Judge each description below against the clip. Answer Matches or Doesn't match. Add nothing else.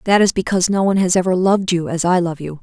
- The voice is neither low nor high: Matches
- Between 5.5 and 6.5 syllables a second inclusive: Doesn't match